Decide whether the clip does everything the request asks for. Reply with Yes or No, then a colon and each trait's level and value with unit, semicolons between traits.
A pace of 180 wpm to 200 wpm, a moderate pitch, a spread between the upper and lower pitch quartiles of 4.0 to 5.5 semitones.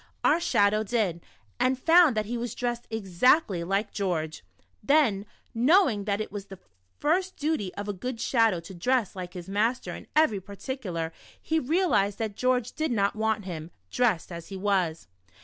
No: average, 185 wpm; high, 215 Hz; average, 4.7 semitones